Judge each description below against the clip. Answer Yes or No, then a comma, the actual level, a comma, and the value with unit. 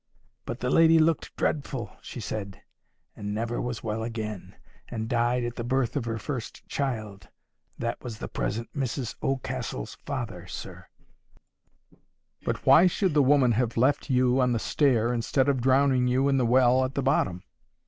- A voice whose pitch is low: Yes, low, 125 Hz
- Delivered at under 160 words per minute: No, average, 170 wpm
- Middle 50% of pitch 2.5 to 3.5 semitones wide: Yes, average, 2.8 semitones